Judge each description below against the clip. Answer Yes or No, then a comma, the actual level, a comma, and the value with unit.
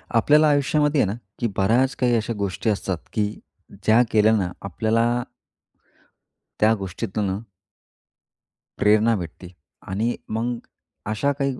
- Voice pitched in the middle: No, low, 110 Hz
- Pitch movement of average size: Yes, average, 3.2 semitones